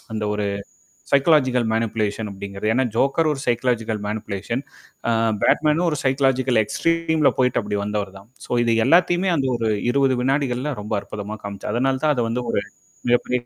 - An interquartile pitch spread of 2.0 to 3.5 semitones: No, average, 4.3 semitones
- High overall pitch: No, low, 125 Hz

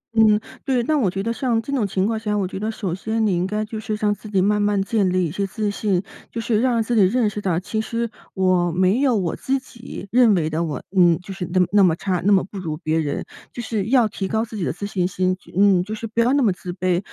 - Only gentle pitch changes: No, average, 3.3 semitones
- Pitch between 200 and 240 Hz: Yes, high, 205 Hz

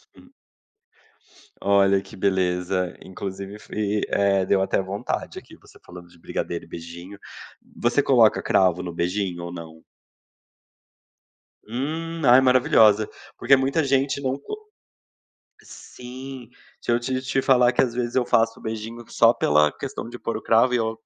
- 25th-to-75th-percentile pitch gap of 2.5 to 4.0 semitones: No, average, 5.2 semitones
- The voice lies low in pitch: Yes, low, 110 Hz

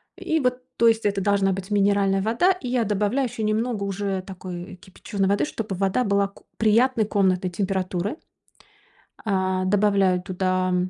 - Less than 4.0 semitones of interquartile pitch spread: Yes, average, 2.7 semitones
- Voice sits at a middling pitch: No, high, 200 Hz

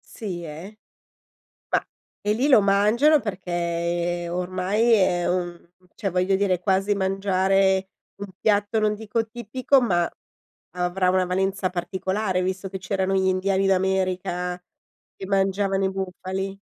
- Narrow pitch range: Yes, narrow, 1.8 semitones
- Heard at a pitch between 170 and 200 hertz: Yes, high, 190 Hz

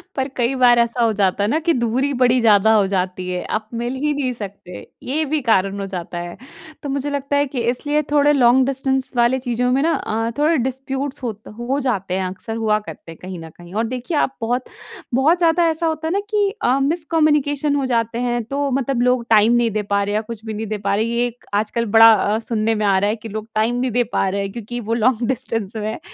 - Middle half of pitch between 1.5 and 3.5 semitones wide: No, average, 4.0 semitones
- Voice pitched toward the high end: Yes, high, 240 Hz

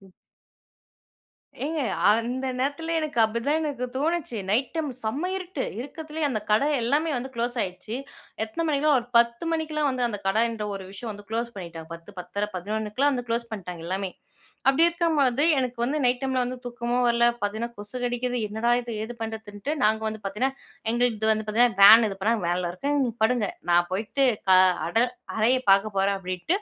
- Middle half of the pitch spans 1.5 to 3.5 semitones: No, average, 4.3 semitones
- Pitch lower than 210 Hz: No, high, 235 Hz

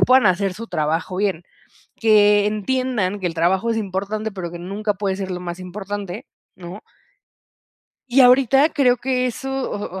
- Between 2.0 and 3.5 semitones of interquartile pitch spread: No, average, 4.0 semitones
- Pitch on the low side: No, high, 205 Hz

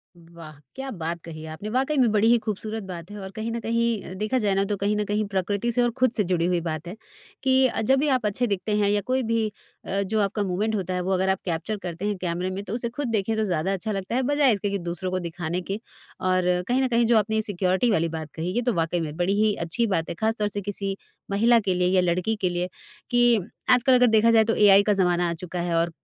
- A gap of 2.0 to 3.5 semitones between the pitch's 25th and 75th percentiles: No, average, 3.9 semitones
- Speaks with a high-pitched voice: Yes, high, 200 Hz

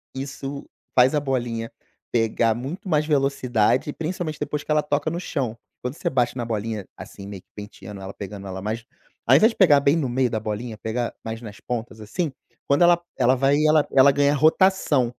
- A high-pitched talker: No, low, 130 Hz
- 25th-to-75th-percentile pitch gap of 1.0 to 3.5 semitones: No, average, 4.7 semitones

